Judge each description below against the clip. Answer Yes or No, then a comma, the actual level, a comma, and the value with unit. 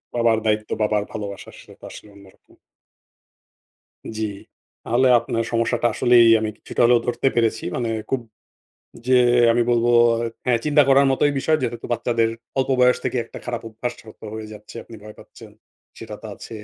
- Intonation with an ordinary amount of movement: No, narrow, 1.9 semitones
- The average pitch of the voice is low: Yes, low, 115 Hz